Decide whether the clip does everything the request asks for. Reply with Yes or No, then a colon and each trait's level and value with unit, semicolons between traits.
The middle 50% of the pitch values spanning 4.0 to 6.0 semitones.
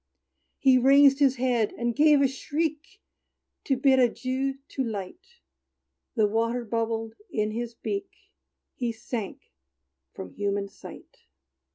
No: average, 3.5 semitones